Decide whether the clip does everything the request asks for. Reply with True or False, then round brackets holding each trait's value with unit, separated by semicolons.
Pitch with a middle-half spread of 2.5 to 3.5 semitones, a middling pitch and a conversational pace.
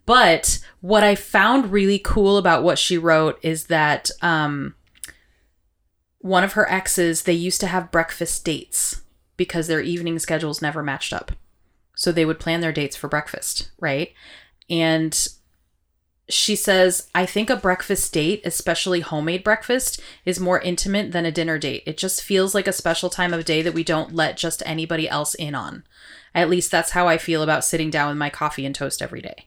True (3.0 semitones; 165 Hz; 185 wpm)